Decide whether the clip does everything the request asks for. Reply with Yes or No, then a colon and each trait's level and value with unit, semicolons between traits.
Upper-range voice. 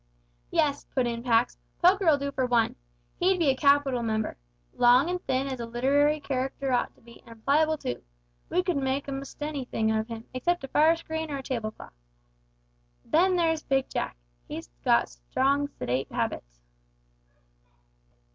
Yes: very high, 270 Hz